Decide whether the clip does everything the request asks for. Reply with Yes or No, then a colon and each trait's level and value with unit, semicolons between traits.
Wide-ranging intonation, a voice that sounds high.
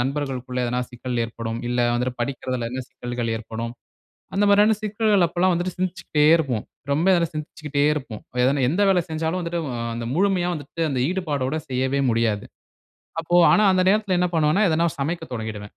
No: wide, 6.3 semitones; medium, 145 Hz